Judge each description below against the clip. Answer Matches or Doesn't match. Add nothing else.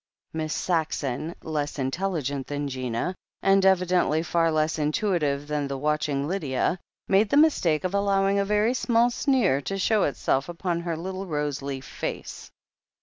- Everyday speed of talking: Matches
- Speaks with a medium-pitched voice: Matches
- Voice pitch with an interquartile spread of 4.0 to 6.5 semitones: Matches